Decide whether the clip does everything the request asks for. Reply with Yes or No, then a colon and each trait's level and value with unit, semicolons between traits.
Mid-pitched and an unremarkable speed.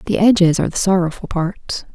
Yes: medium, 180 Hz; average, 185 wpm